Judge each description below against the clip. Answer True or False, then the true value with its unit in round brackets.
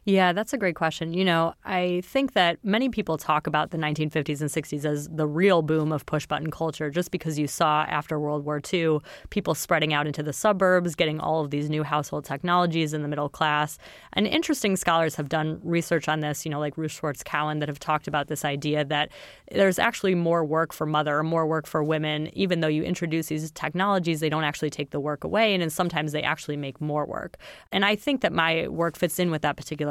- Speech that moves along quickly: True (230 wpm)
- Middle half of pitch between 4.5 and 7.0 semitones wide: False (2.8 semitones)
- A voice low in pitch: False (155 Hz)